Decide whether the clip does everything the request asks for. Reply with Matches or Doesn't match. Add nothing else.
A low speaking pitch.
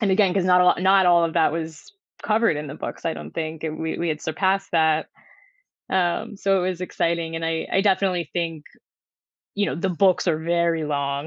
Doesn't match